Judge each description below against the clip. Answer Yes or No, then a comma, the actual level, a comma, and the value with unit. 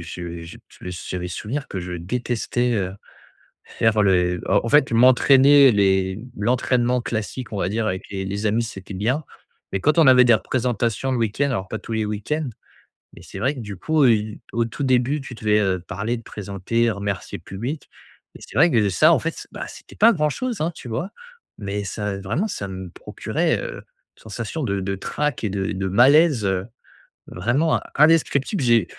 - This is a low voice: Yes, low, 115 Hz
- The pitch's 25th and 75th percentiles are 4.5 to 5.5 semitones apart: Yes, average, 5.1 semitones